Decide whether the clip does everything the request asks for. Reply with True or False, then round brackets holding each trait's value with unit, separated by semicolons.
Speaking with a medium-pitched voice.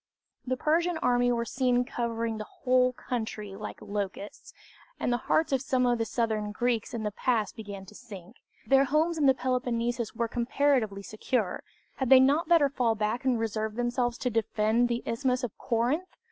False (240 Hz)